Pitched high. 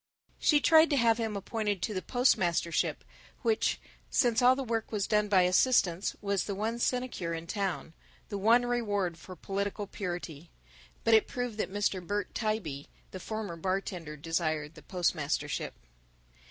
Yes: high, 200 Hz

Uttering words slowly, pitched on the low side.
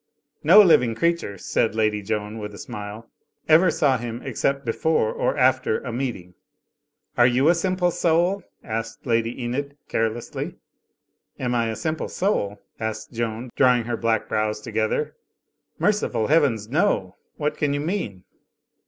No: average, 150 wpm; low, 120 Hz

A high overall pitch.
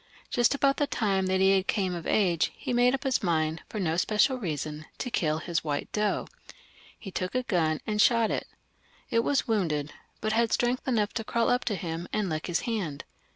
Yes: high, 200 Hz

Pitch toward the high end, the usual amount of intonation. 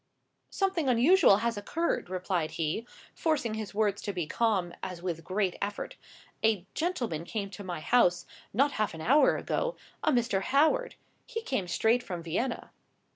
No: high, 215 Hz; wide, 6.4 semitones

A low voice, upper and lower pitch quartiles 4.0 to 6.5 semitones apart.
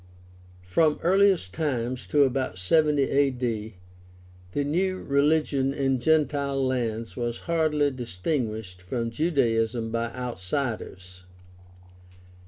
Yes: low, 130 Hz; average, 4.6 semitones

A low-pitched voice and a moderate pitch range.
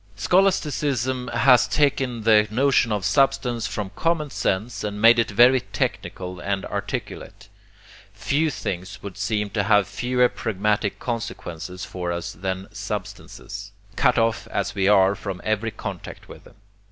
Yes: low, 105 Hz; average, 4.0 semitones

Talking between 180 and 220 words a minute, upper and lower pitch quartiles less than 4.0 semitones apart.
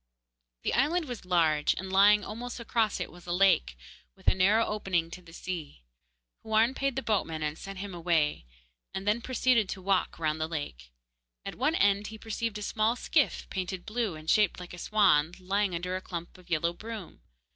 No: average, 195 wpm; average, 4.4 semitones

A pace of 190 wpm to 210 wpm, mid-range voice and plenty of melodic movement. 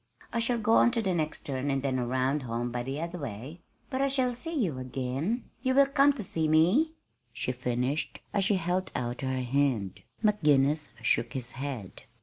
Yes: average, 200 wpm; medium, 145 Hz; wide, 8.7 semitones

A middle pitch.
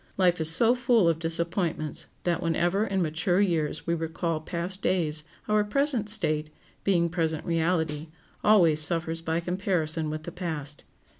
Yes: medium, 170 Hz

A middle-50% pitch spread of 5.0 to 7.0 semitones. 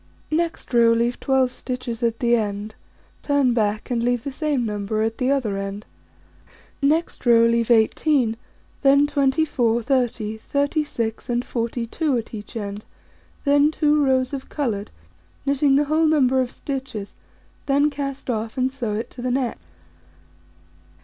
No: average, 3.7 semitones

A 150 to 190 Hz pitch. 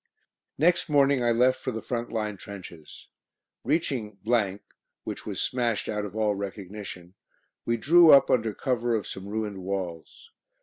No: low, 110 Hz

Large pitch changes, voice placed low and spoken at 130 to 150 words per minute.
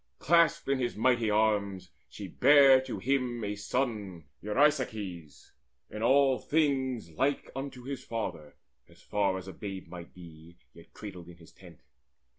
Yes: wide, 6.2 semitones; low, 110 Hz; average, 140 wpm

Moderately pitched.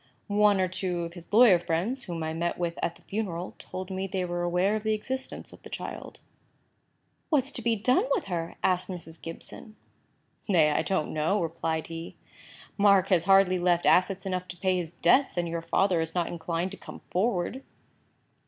Yes: medium, 180 Hz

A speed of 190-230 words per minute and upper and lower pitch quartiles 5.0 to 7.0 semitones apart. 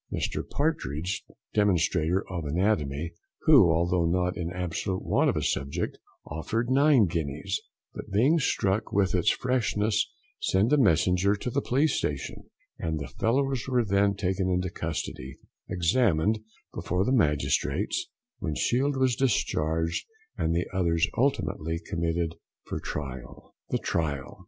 No: slow, 135 wpm; wide, 5.4 semitones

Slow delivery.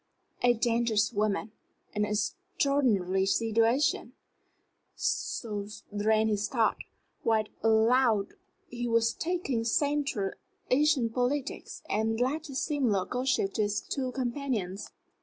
Yes: slow, 110 wpm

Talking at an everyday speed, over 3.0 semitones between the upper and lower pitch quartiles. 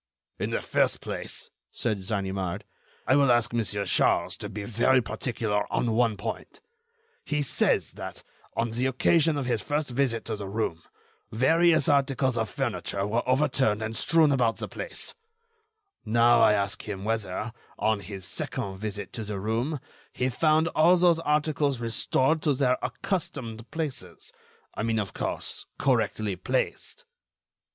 Yes: average, 150 wpm; average, 4.8 semitones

